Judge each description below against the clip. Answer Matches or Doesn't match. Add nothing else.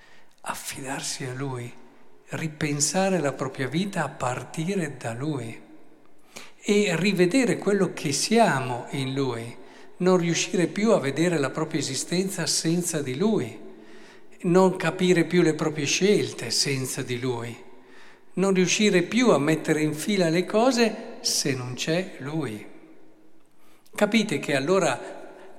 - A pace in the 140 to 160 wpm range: Doesn't match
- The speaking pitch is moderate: Matches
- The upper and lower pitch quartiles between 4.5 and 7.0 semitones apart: Matches